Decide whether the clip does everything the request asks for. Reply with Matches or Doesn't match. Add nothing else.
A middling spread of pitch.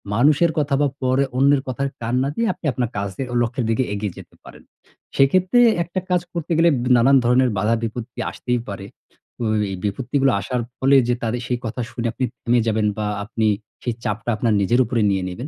Matches